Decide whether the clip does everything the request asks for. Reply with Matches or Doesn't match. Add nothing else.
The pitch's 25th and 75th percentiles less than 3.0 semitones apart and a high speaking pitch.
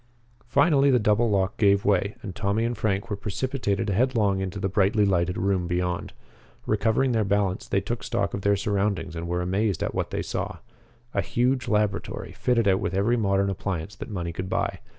Doesn't match